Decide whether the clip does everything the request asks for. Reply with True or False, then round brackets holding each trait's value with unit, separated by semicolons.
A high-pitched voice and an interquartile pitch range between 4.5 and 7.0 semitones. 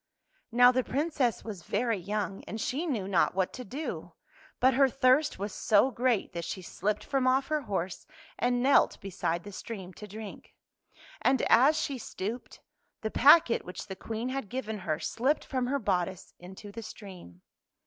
True (225 Hz; 5.0 semitones)